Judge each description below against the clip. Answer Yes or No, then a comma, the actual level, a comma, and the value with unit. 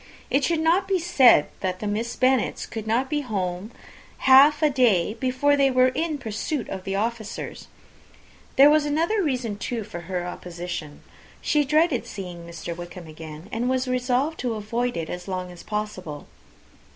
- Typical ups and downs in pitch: No, wide, 7.1 semitones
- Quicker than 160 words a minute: Yes, average, 170 wpm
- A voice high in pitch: Yes, high, 235 Hz